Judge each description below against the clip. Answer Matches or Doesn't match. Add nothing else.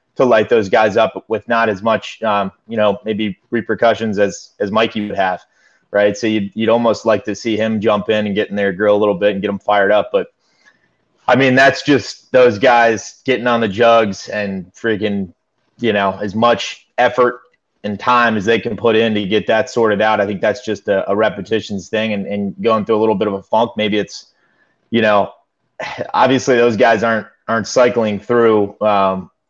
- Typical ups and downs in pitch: Doesn't match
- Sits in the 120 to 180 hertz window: Doesn't match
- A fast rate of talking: Matches